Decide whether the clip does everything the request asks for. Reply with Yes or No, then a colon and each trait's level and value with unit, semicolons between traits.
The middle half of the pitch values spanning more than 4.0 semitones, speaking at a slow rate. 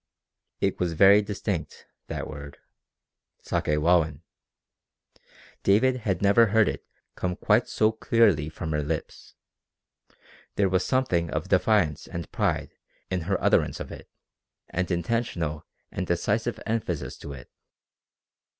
Yes: average, 4.9 semitones; slow, 125 wpm